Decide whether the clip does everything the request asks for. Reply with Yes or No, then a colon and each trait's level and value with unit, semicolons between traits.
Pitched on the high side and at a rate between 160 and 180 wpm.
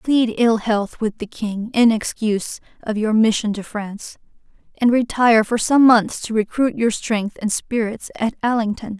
Yes: high, 220 Hz; average, 175 wpm